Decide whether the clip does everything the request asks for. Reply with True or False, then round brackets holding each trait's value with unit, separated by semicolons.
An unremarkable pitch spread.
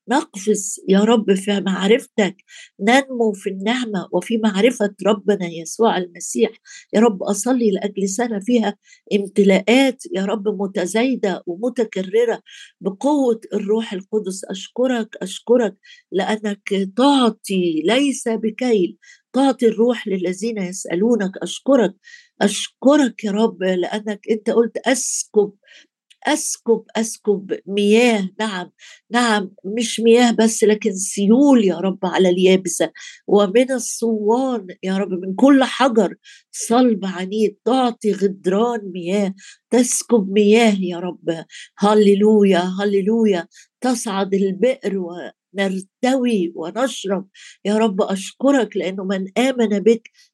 True (3.6 semitones)